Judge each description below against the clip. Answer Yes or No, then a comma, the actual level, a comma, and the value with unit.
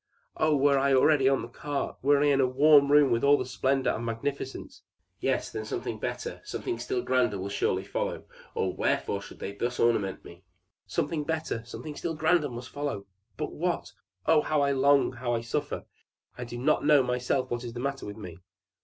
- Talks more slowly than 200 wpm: No, fast, 205 wpm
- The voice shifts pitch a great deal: No, average, 3.6 semitones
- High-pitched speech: No, low, 135 Hz